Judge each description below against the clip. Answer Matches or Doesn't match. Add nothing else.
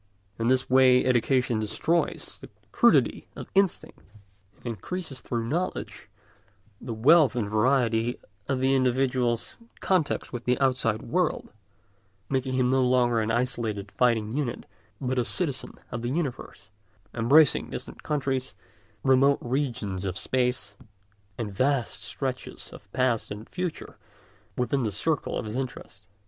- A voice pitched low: Matches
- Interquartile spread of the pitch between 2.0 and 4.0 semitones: Matches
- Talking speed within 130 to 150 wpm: Matches